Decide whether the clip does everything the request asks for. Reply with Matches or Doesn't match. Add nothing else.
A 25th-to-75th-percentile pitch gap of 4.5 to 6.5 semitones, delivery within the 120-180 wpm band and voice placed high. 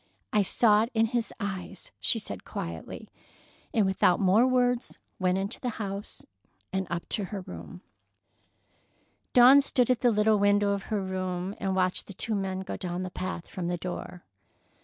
Doesn't match